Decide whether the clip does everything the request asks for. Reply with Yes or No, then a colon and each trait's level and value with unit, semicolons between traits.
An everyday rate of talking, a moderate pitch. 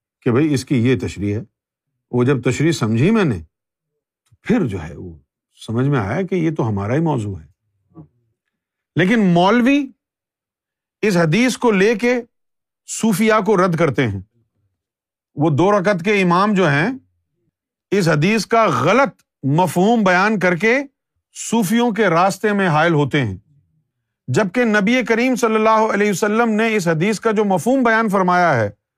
Yes: average, 160 wpm; medium, 175 Hz